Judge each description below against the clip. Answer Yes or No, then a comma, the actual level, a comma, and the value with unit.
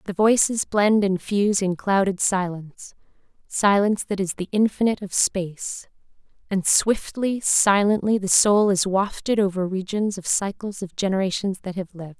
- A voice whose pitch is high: Yes, high, 195 Hz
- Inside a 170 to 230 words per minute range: No, average, 155 wpm